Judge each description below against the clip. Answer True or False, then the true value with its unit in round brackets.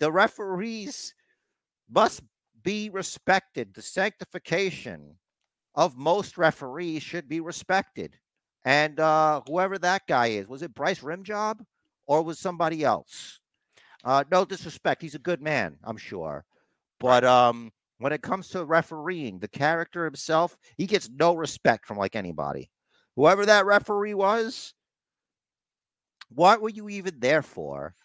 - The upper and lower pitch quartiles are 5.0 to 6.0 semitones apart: True (5.6 semitones)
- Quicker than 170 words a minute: False (135 wpm)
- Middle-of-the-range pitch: True (165 Hz)